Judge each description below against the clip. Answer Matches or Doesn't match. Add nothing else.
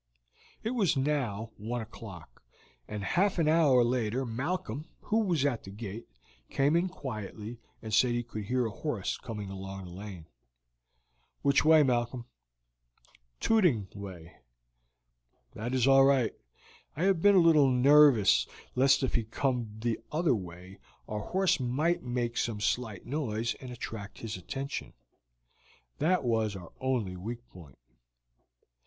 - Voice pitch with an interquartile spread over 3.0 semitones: Matches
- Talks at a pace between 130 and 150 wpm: Matches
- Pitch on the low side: Matches